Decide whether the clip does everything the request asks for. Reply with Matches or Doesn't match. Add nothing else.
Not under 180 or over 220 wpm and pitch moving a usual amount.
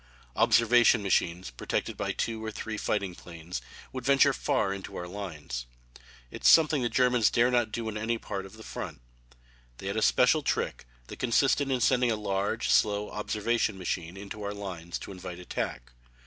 Matches